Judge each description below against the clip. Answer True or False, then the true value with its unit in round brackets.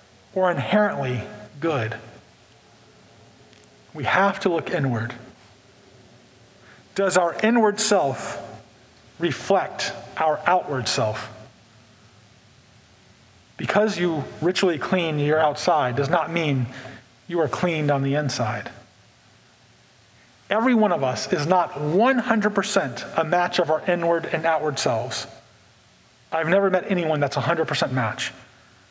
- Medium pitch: True (145 Hz)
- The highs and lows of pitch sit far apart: True (7.2 semitones)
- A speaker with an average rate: False (110 wpm)